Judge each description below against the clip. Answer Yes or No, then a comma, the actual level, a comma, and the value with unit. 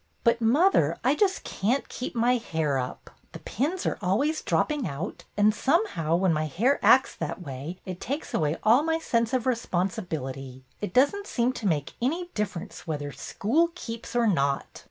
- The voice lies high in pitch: Yes, high, 220 Hz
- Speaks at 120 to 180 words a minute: No, average, 190 wpm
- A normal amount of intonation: No, wide, 8.5 semitones